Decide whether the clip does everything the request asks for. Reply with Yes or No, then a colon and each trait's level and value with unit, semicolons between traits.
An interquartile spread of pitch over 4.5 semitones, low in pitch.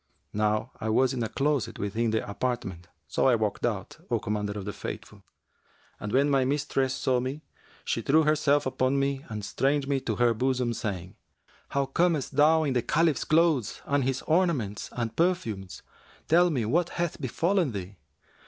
Yes: average, 5.2 semitones; low, 130 Hz